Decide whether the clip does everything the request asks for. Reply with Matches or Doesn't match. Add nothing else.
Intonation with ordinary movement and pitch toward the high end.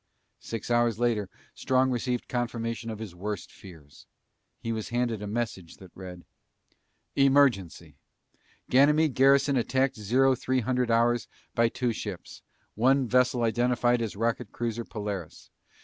Doesn't match